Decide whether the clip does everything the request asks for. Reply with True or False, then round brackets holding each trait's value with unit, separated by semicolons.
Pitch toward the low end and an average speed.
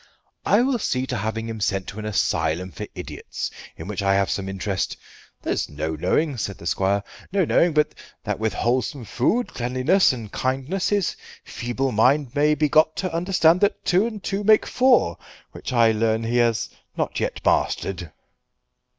True (120 Hz; 175 wpm)